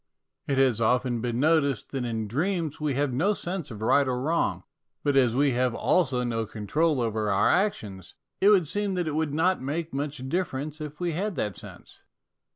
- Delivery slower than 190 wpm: No, average, 195 wpm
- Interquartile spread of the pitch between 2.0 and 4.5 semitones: No, average, 5.1 semitones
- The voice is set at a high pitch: No, medium, 140 Hz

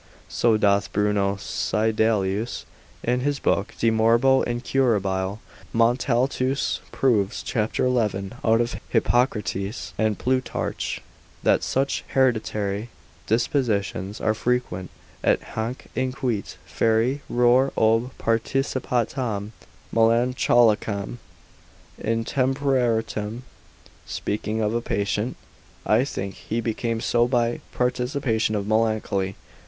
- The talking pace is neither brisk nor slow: No, slow, 95 wpm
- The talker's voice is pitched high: No, low, 115 Hz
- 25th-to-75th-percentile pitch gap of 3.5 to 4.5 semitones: No, average, 2.8 semitones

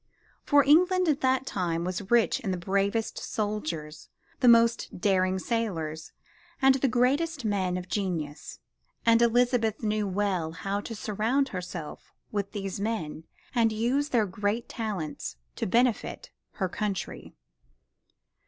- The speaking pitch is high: Yes, high, 210 Hz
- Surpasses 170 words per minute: No, slow, 135 wpm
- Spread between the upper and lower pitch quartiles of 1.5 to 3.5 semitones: No, average, 4.5 semitones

